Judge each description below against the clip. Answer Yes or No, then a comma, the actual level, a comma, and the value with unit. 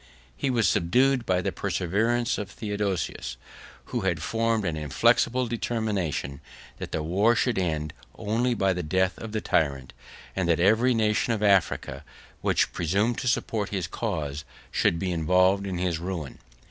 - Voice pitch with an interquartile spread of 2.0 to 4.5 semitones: No, average, 5.0 semitones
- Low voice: Yes, very low, 95 Hz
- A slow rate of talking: No, average, 160 wpm